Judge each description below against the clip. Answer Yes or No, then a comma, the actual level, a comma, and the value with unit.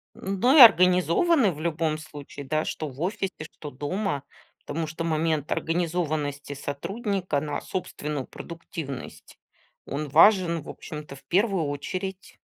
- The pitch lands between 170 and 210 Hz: No, medium, 160 Hz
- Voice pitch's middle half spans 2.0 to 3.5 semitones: No, average, 4.1 semitones